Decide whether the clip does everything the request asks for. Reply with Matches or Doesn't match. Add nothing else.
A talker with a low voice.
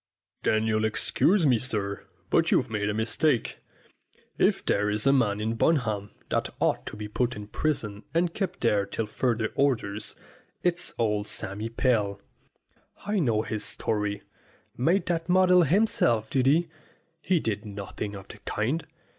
Matches